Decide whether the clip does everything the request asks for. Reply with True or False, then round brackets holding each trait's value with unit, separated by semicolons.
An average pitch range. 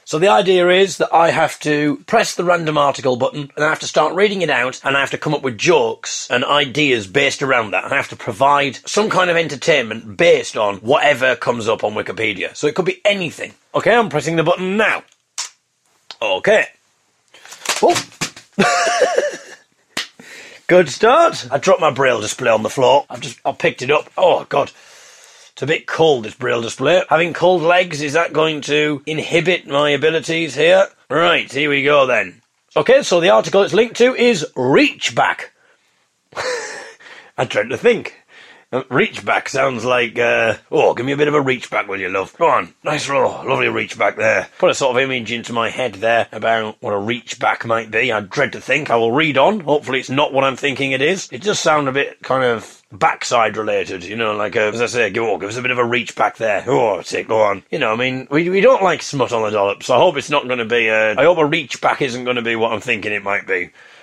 False (7.0 semitones)